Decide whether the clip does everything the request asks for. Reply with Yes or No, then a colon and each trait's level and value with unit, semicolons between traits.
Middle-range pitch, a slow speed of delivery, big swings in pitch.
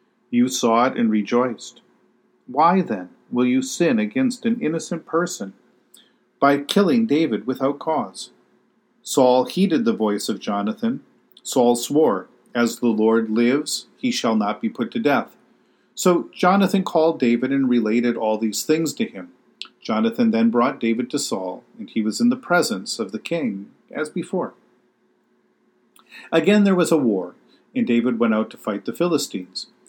No: medium, 150 Hz; average, 160 wpm; wide, 8.8 semitones